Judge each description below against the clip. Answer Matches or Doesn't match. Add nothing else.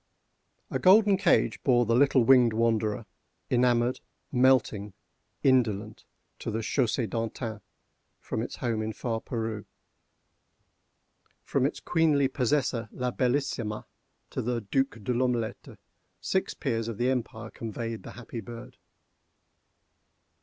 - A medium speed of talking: Doesn't match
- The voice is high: Doesn't match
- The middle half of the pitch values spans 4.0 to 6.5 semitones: Doesn't match